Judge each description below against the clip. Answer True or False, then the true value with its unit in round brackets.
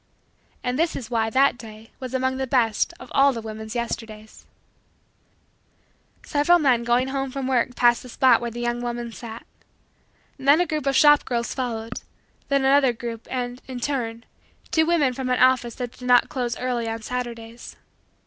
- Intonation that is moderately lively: False (2.3 semitones)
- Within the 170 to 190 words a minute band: True (175 wpm)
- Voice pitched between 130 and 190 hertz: False (245 Hz)